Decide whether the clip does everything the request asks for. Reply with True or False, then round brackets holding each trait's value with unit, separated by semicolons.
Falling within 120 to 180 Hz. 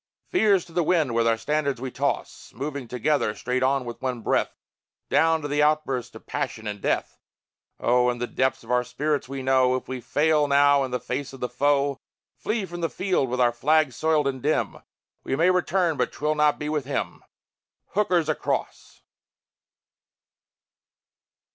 True (140 Hz)